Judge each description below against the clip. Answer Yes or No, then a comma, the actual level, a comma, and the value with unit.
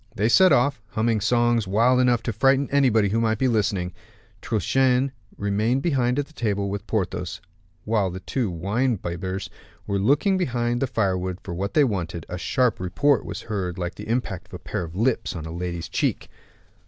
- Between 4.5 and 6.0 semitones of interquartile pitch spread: Yes, average, 5.2 semitones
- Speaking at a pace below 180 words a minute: No, average, 185 wpm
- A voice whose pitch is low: Yes, low, 110 Hz